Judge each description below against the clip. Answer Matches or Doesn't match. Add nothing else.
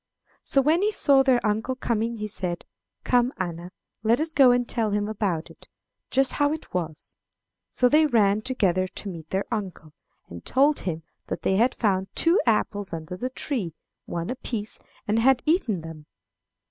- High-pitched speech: Matches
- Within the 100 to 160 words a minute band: Doesn't match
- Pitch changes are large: Matches